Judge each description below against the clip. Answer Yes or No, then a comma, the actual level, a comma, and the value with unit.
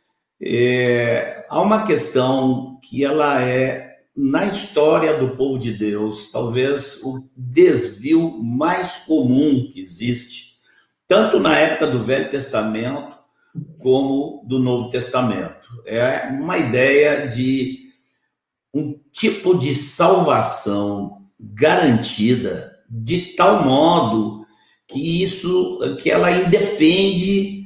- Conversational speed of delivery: No, slow, 100 wpm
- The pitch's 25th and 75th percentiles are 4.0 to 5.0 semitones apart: Yes, average, 4.7 semitones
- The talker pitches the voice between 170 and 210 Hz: No, low, 135 Hz